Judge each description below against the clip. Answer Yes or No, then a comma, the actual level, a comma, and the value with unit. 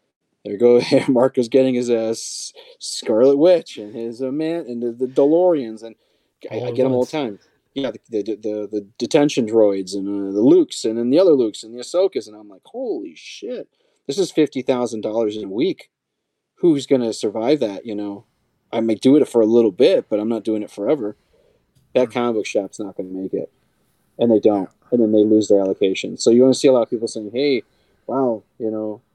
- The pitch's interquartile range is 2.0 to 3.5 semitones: No, average, 4.0 semitones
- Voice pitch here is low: Yes, low, 120 Hz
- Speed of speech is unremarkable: No, fast, 220 wpm